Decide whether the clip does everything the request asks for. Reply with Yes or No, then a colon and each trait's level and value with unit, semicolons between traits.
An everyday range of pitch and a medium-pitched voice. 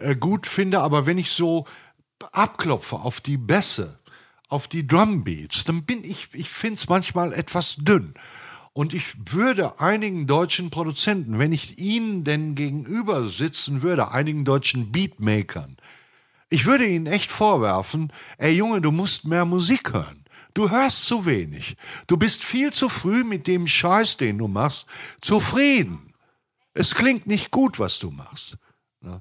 No: wide, 6.2 semitones; medium, 170 Hz